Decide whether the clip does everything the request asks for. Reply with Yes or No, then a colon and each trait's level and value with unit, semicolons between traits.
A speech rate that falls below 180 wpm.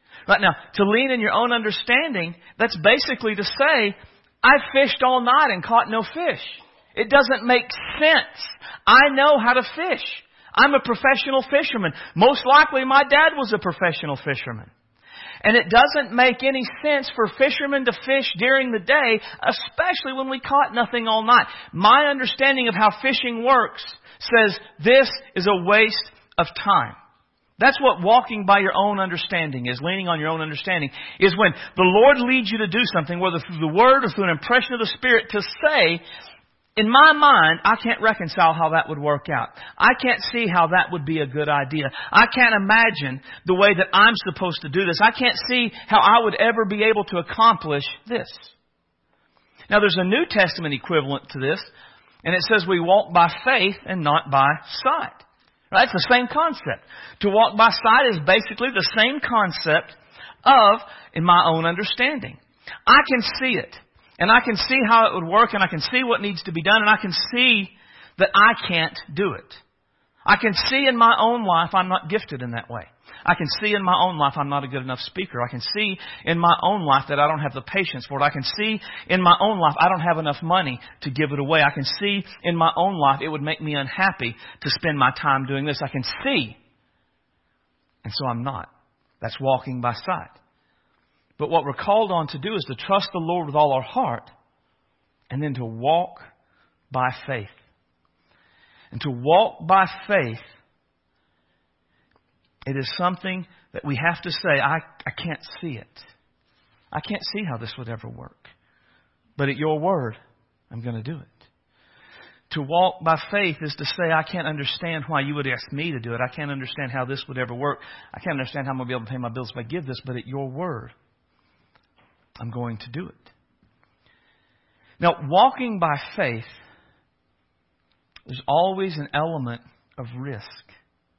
No: average, 195 wpm